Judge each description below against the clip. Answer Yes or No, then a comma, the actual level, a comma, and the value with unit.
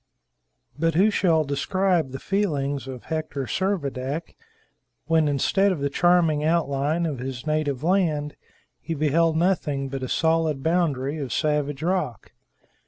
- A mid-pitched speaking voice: Yes, medium, 155 Hz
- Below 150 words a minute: Yes, slow, 135 wpm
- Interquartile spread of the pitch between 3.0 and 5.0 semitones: Yes, average, 3.4 semitones